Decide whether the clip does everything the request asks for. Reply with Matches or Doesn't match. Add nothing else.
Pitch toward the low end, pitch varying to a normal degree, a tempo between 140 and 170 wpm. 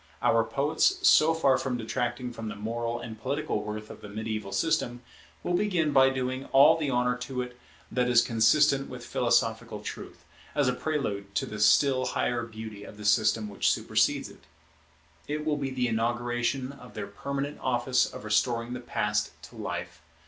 Doesn't match